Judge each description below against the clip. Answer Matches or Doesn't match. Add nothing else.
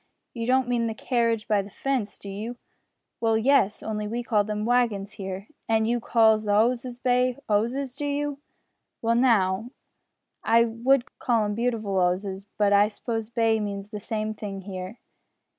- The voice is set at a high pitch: Matches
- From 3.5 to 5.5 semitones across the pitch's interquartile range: Doesn't match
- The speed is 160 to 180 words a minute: Matches